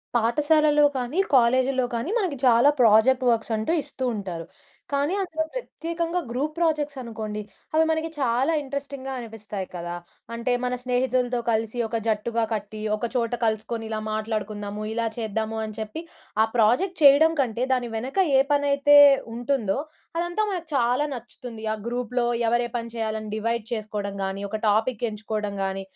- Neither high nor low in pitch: No, high, 235 Hz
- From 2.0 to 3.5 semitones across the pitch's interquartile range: No, average, 4.3 semitones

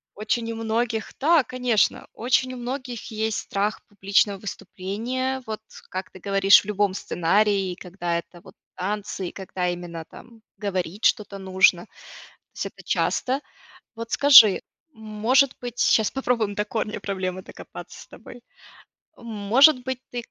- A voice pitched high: Yes, high, 210 Hz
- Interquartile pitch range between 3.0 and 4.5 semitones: Yes, average, 3.8 semitones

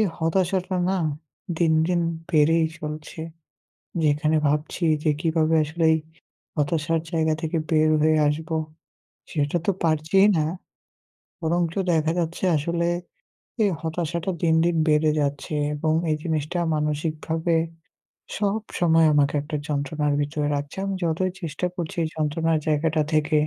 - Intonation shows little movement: Yes, narrow, 1.9 semitones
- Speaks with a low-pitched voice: No, medium, 160 Hz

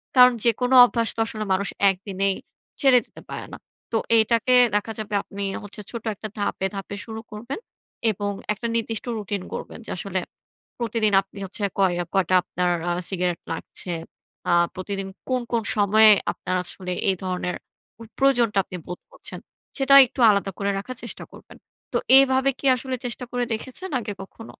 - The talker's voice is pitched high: Yes, high, 215 Hz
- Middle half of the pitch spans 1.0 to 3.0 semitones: No, average, 3.6 semitones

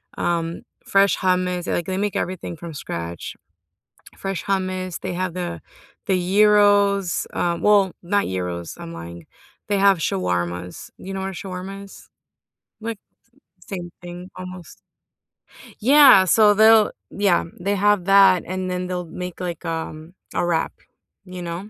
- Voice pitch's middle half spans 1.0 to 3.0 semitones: Yes, narrow, 2.5 semitones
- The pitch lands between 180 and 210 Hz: Yes, medium, 185 Hz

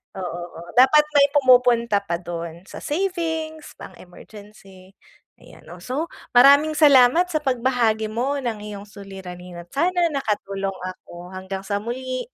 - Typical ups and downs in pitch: No, wide, 6.6 semitones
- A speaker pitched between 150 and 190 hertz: No, high, 235 Hz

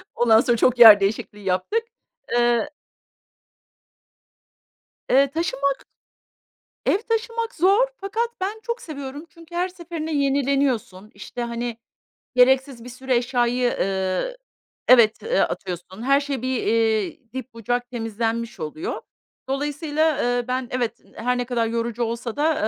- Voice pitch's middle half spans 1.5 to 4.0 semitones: No, average, 4.6 semitones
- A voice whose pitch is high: Yes, very high, 255 Hz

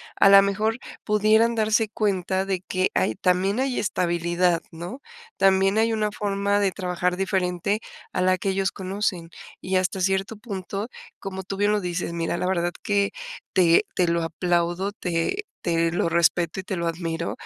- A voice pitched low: No, high, 190 Hz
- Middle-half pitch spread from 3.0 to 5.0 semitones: No, narrow, 2.6 semitones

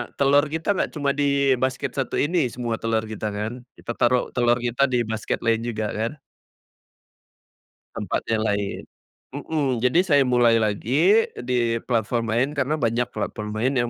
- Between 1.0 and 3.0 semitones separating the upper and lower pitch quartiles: No, average, 3.6 semitones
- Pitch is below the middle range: Yes, low, 120 Hz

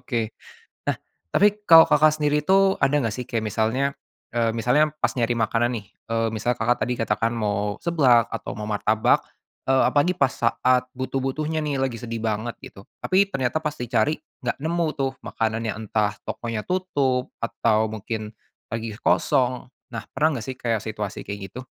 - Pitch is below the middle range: Yes, low, 120 Hz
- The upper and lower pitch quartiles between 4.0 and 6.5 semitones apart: Yes, average, 4.4 semitones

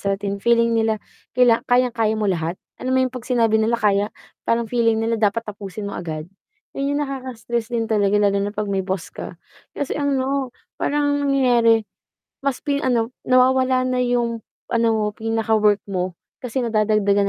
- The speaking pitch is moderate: No, high, 230 Hz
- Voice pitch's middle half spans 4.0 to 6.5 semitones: No, average, 3.4 semitones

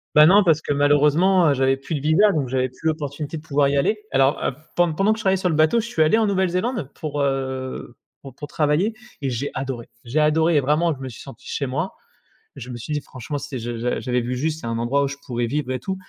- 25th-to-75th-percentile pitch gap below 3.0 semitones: No, average, 3.5 semitones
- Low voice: No, medium, 145 Hz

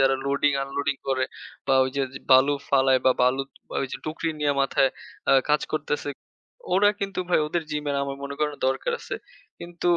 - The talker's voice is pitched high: No, medium, 140 Hz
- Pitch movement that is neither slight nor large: No, narrow, 2.1 semitones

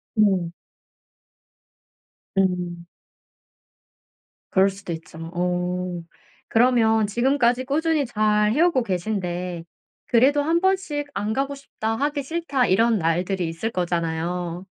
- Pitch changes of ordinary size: No, wide, 6.9 semitones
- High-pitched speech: Yes, high, 210 Hz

